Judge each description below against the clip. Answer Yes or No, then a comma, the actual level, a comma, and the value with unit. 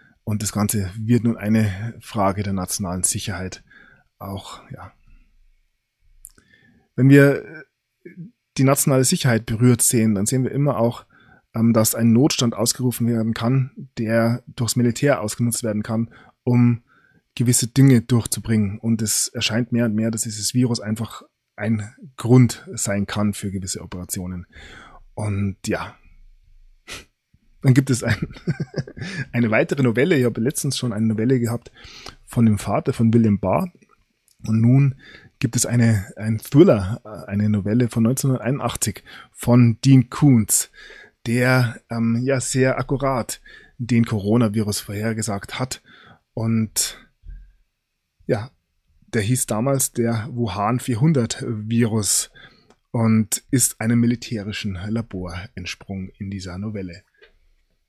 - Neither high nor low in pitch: No, low, 115 Hz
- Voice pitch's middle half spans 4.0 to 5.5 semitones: No, average, 2.9 semitones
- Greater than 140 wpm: No, slow, 125 wpm